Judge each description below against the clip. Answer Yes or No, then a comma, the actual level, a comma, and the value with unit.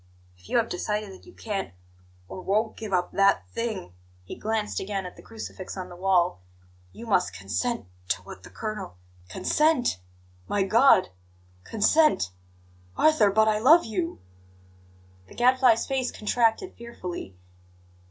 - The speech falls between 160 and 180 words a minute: No, average, 145 wpm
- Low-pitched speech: No, high, 210 Hz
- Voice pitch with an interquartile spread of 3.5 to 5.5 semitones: Yes, average, 4.4 semitones